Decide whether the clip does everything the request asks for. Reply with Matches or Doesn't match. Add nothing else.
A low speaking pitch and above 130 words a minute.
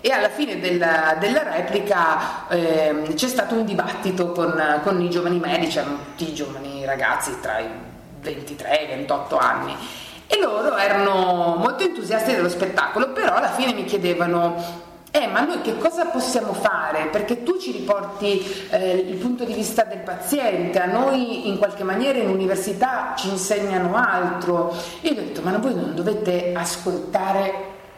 Doesn't match